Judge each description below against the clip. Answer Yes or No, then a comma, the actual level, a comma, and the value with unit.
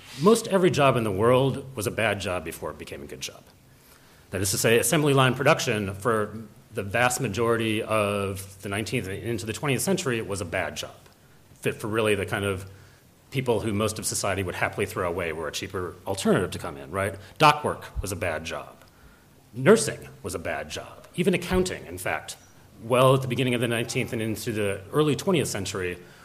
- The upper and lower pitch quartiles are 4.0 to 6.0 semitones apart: Yes, average, 4.5 semitones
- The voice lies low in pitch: Yes, low, 115 Hz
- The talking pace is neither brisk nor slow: No, fast, 210 wpm